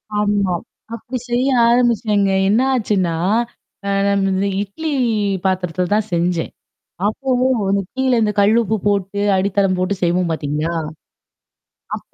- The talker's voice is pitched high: Yes, high, 200 Hz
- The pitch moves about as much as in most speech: Yes, average, 3.2 semitones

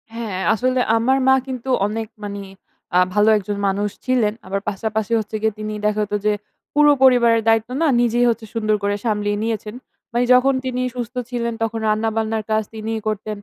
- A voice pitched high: Yes, high, 220 Hz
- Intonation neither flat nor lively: No, narrow, 2.2 semitones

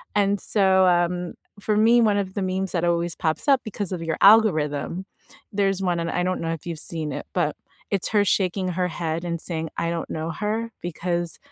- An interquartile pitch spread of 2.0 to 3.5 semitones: Yes, average, 2.9 semitones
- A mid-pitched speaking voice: Yes, medium, 180 Hz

